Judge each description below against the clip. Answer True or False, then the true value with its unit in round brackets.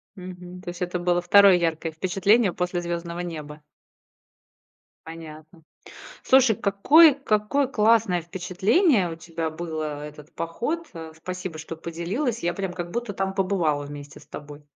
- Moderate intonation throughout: True (3.6 semitones)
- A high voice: False (175 Hz)